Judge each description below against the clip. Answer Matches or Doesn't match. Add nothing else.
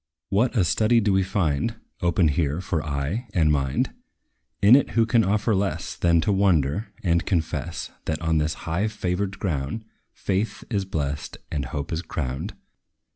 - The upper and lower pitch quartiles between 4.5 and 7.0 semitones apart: Matches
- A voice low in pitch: Matches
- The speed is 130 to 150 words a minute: Doesn't match